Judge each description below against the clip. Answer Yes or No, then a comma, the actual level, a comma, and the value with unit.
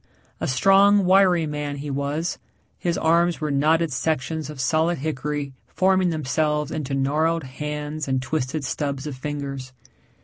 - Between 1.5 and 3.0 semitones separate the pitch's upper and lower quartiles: Yes, average, 2.7 semitones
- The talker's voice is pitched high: No, medium, 150 Hz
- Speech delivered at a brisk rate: No, average, 140 wpm